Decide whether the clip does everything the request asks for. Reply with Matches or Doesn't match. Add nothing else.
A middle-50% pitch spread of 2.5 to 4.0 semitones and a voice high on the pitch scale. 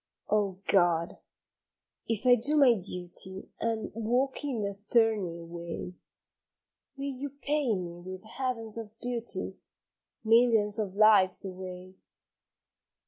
Doesn't match